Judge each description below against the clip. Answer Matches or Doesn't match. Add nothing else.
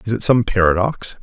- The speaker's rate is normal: Matches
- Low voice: Matches